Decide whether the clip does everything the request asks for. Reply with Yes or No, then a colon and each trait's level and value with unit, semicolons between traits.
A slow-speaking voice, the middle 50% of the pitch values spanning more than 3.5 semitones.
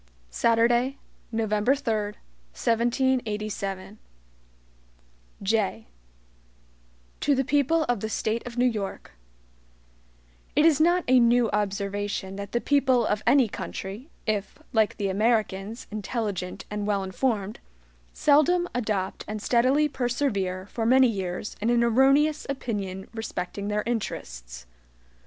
Yes: slow, 115 wpm; average, 4.0 semitones